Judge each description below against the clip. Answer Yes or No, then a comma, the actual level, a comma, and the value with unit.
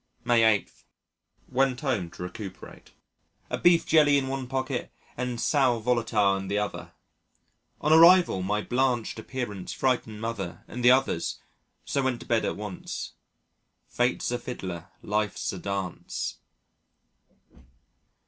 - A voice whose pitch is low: Yes, low, 120 Hz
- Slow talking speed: Yes, slow, 130 wpm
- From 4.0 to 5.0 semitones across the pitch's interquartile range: Yes, average, 4.3 semitones